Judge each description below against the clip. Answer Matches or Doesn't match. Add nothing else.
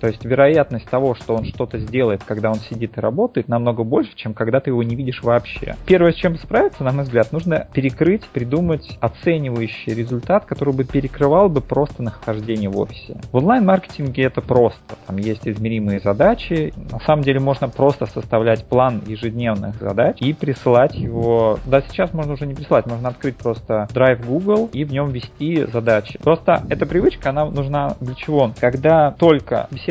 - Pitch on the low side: Matches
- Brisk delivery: Matches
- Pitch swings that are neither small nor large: Matches